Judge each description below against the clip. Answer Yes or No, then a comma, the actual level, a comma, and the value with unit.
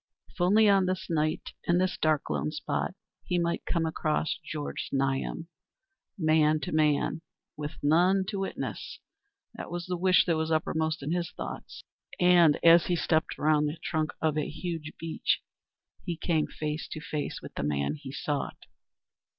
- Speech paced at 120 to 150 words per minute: No, average, 165 wpm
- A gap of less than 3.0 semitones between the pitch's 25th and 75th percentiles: Yes, narrow, 2.5 semitones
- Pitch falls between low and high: Yes, medium, 160 Hz